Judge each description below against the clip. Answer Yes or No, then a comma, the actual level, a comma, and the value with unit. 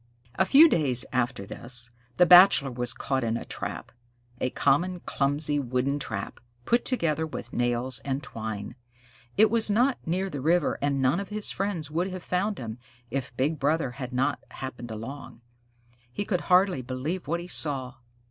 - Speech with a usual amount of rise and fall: No, wide, 6.1 semitones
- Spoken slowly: No, average, 170 wpm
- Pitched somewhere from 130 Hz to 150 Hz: Yes, medium, 140 Hz